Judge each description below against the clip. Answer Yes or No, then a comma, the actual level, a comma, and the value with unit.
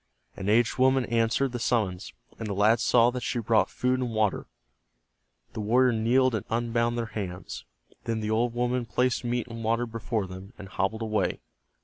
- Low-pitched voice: Yes, low, 115 Hz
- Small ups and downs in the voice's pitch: Yes, narrow, 2.2 semitones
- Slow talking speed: No, average, 180 wpm